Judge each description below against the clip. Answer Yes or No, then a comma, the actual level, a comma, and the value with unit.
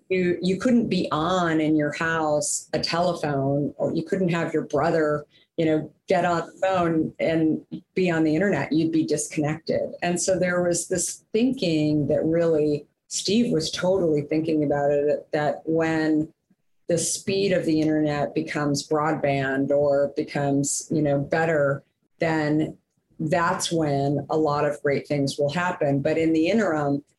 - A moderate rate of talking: Yes, average, 160 wpm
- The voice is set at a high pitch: No, medium, 155 Hz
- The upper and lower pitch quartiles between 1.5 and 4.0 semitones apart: Yes, narrow, 2.6 semitones